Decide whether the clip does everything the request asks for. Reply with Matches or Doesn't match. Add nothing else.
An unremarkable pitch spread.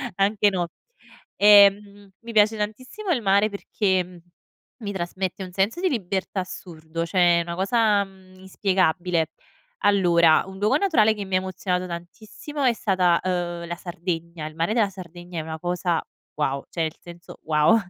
Matches